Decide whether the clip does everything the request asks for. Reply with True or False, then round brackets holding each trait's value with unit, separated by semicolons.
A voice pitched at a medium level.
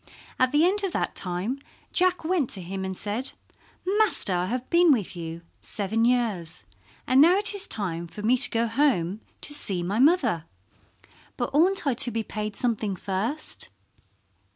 False (230 Hz)